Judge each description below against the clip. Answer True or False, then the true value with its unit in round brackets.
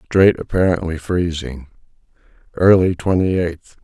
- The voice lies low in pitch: True (85 Hz)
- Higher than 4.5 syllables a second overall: False (4.3 syllables/s)